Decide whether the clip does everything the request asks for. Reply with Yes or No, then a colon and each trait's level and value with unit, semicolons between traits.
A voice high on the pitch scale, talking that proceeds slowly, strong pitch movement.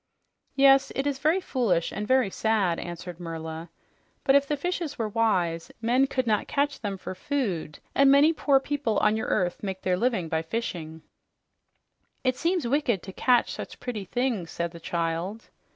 No: high, 220 Hz; average, 175 wpm; wide, 7.5 semitones